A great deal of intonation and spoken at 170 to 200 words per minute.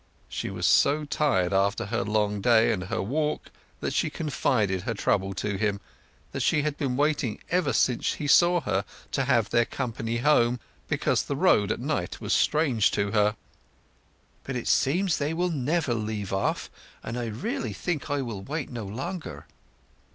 Yes: wide, 6.1 semitones; average, 175 wpm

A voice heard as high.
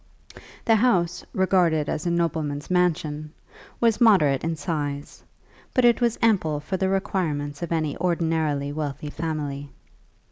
No: medium, 165 Hz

